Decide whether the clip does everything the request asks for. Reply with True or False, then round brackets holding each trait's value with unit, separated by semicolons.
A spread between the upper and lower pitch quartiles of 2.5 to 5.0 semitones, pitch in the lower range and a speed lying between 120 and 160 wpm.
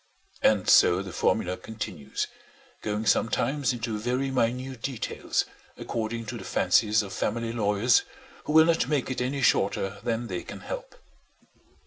True (3.3 semitones; 115 Hz; 145 wpm)